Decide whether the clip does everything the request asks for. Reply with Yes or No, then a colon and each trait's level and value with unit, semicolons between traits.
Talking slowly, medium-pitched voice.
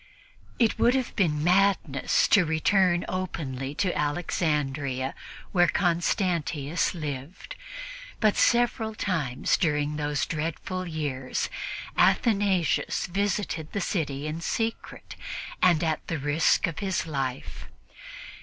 Yes: slow, 105 wpm; medium, 165 Hz